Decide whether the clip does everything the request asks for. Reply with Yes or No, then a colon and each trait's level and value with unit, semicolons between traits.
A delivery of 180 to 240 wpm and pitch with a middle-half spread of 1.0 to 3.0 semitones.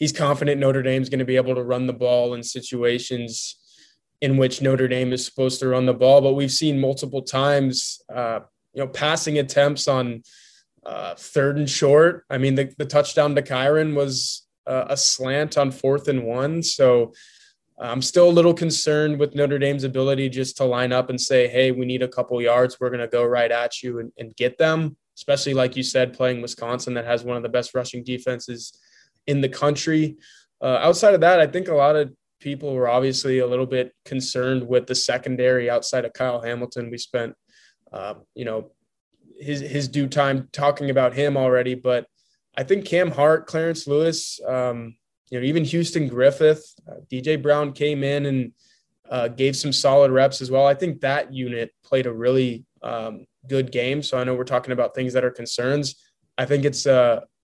Yes: average, 200 wpm; narrow, 2.5 semitones